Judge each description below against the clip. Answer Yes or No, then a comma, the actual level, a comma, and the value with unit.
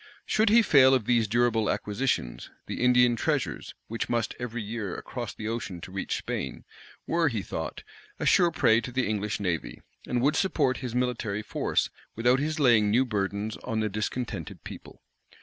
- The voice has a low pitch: Yes, low, 120 Hz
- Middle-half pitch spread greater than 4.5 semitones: No, average, 3.2 semitones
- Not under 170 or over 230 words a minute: Yes, average, 175 wpm